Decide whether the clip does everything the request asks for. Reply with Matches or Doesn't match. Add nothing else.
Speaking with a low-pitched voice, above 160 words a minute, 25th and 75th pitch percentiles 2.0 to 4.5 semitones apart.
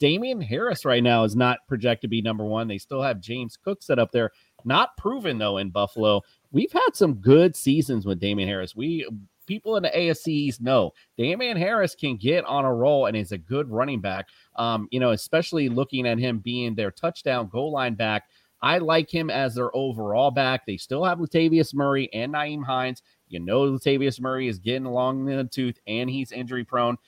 Matches